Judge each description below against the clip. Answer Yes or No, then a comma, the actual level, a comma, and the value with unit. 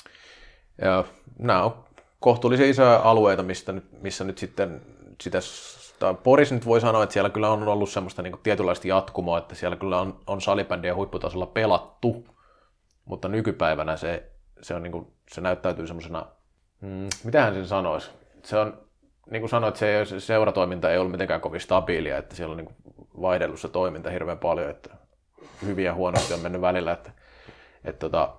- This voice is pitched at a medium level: No, very low, 95 Hz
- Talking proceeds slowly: No, fast, 155 wpm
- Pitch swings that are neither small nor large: Yes, average, 3.1 semitones